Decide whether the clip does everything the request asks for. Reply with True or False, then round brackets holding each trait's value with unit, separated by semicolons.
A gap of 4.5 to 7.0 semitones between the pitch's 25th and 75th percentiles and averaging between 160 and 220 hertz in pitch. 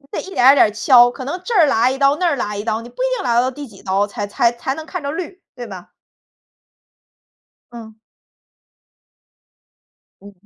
False (4.9 semitones; 245 Hz)